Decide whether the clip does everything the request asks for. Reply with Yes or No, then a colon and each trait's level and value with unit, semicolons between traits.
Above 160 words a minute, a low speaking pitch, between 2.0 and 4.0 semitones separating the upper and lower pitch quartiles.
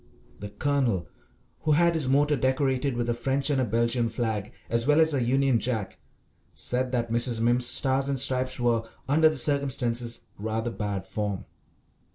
Yes: average, 170 wpm; low, 125 Hz; average, 2.8 semitones